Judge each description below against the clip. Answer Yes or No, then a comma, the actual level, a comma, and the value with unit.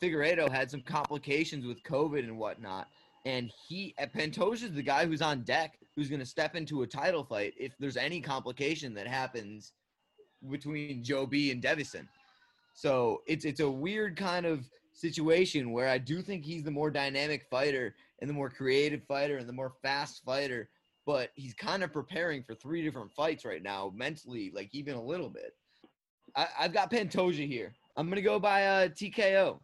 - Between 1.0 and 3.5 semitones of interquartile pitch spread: No, average, 3.9 semitones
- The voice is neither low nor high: Yes, medium, 145 Hz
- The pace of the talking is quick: No, average, 190 wpm